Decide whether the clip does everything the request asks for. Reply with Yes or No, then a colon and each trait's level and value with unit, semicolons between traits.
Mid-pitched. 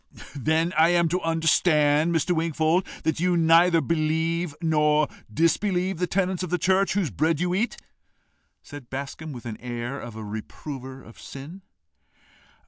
Yes: medium, 160 Hz